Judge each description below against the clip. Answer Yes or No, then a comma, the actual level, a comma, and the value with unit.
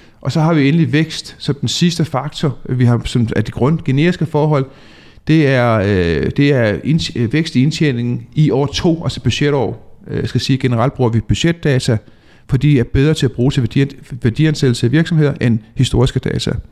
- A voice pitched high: No, low, 135 Hz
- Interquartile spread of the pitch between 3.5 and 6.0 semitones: Yes, average, 3.8 semitones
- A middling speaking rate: Yes, average, 195 wpm